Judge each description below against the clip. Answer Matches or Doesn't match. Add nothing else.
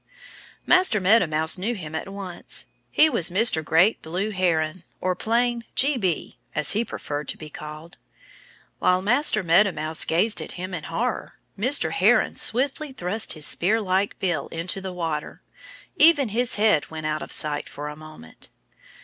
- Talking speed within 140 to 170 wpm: Matches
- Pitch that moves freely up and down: Matches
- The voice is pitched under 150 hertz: Doesn't match